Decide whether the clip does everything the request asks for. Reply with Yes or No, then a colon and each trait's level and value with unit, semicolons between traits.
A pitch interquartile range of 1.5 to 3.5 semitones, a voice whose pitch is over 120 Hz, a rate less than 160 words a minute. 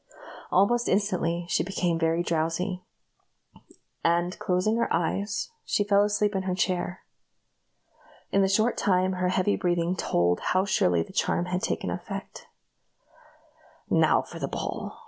Yes: narrow, 2.6 semitones; medium, 185 Hz; average, 140 wpm